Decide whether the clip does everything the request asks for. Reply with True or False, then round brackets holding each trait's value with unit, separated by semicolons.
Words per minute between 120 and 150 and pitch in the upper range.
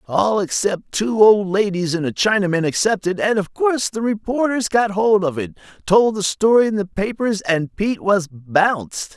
False (185 wpm; 200 Hz)